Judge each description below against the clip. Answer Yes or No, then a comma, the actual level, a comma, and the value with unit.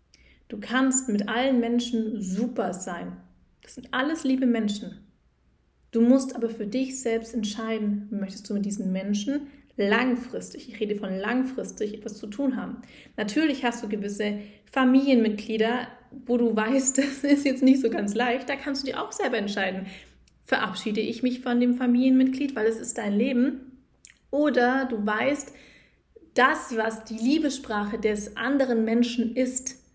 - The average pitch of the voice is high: Yes, high, 235 Hz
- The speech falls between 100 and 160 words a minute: Yes, average, 155 wpm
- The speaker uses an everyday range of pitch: Yes, average, 3.5 semitones